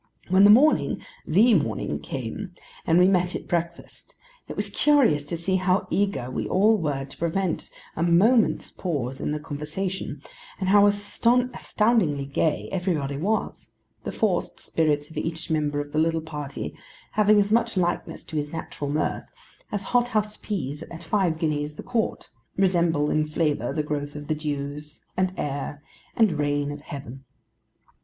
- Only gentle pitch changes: No, average, 5.1 semitones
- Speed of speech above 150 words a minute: Yes, average, 160 wpm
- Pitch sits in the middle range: Yes, medium, 165 Hz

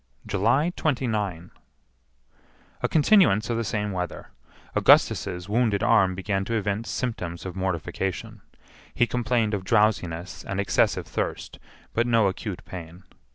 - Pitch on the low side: Yes, low, 105 Hz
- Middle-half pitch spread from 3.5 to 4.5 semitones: Yes, average, 3.8 semitones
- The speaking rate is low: Yes, slow, 125 wpm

